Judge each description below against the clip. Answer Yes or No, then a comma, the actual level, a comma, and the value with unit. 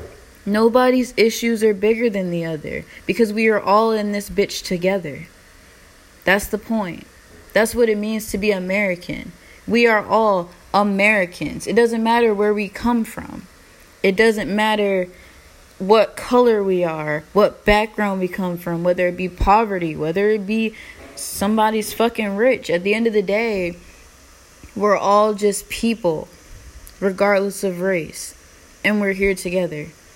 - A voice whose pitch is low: No, high, 200 Hz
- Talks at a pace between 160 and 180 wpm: No, average, 150 wpm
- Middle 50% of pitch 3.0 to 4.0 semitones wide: Yes, average, 3.5 semitones